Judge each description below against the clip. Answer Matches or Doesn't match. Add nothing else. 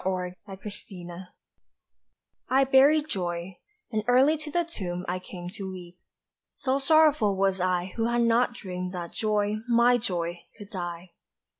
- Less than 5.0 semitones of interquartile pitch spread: Doesn't match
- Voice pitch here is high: Matches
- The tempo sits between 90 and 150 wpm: Matches